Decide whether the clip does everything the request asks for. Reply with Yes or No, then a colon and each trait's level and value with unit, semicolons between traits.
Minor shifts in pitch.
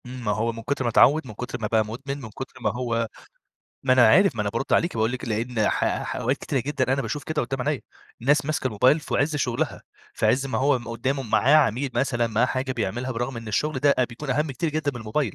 No: average, 3.4 semitones